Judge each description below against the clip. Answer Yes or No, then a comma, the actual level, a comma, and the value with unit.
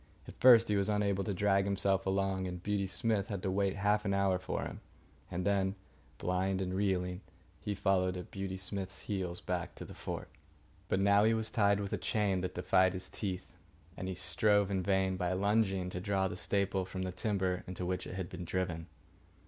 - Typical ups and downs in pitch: No, narrow, 1.6 semitones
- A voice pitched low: Yes, very low, 95 Hz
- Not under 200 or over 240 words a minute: Yes, fast, 205 wpm